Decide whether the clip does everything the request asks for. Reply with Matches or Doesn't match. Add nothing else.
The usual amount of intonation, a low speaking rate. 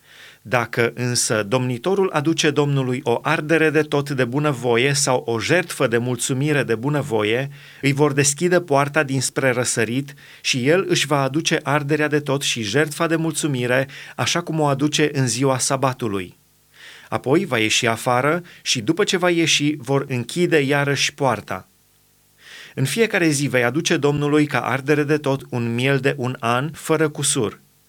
Doesn't match